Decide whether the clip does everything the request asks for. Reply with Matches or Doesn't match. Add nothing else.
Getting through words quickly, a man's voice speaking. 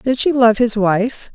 Doesn't match